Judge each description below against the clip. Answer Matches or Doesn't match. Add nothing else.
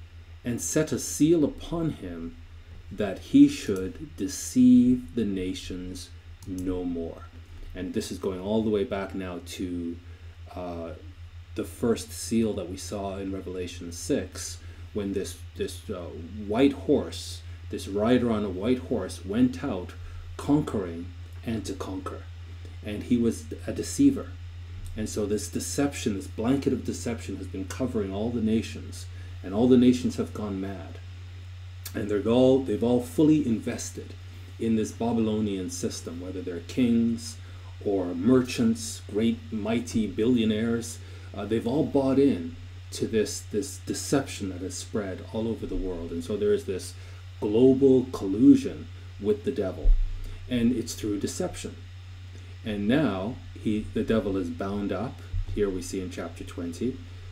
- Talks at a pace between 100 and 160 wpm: Matches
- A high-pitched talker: Doesn't match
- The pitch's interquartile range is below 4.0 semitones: Matches